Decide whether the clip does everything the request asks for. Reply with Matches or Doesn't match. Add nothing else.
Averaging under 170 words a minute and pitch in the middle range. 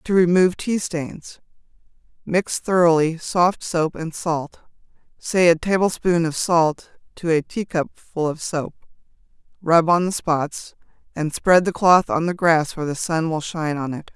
Matches